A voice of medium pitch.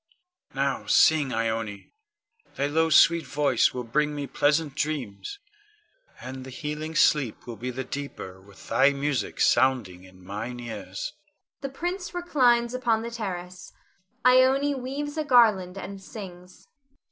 Yes: medium, 150 Hz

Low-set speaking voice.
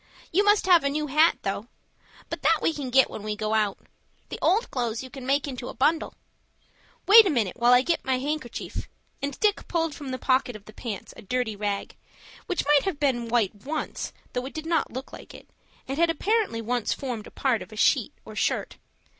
No: very high, 265 Hz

